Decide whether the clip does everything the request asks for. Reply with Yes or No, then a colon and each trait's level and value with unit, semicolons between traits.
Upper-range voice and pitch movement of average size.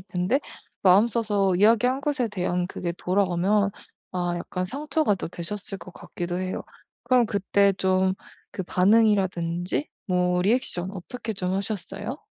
Yes: high, 195 Hz; average, 3.5 semitones